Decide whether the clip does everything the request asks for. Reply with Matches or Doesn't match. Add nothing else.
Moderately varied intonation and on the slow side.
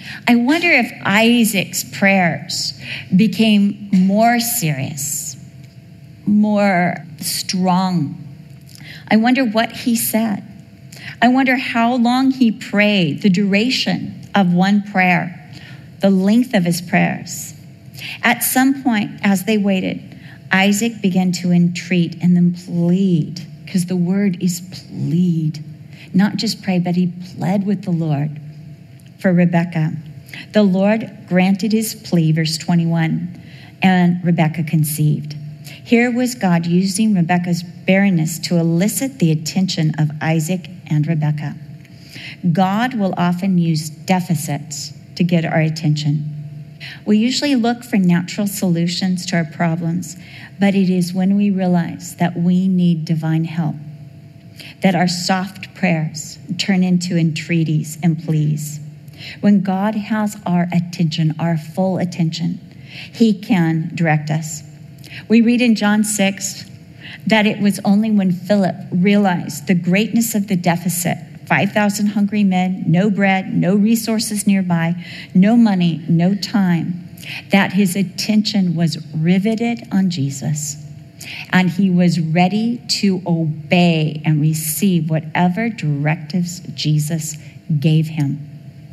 Matches